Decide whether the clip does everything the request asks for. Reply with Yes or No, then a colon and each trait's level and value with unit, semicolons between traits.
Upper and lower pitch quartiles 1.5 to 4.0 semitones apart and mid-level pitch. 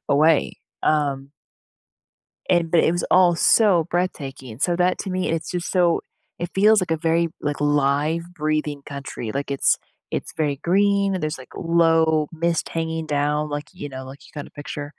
Yes: average, 3.0 semitones; medium, 160 Hz